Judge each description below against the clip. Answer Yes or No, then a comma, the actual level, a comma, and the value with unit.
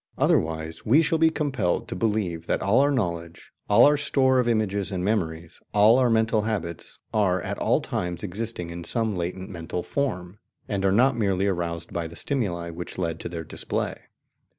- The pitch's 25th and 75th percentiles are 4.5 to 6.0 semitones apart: Yes, average, 5.2 semitones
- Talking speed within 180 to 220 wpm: Yes, average, 185 wpm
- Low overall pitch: Yes, low, 100 Hz